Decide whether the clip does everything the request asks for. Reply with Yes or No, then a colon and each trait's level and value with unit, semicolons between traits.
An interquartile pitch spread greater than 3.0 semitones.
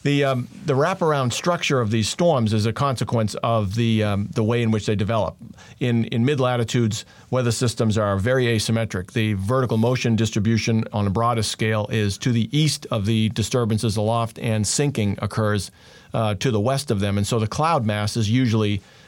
No: narrow, 2.5 semitones